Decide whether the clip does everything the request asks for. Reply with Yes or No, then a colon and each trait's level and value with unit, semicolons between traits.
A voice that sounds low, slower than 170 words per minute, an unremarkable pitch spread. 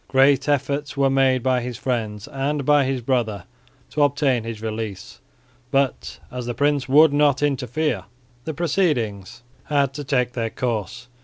Yes: low, 130 Hz; average, 155 wpm; average, 3.4 semitones